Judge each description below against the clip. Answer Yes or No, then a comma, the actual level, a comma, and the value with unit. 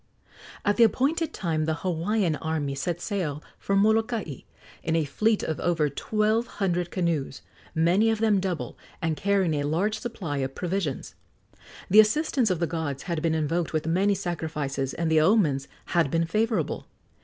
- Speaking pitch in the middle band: Yes, medium, 170 Hz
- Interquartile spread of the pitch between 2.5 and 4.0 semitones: No, average, 4.8 semitones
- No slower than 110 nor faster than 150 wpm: No, average, 165 wpm